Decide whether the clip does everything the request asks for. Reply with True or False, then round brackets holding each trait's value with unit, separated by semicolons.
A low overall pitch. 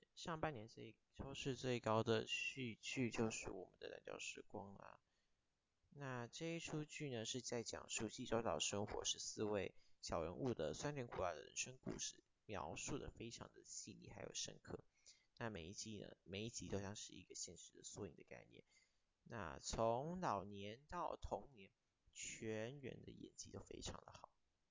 True (115 Hz)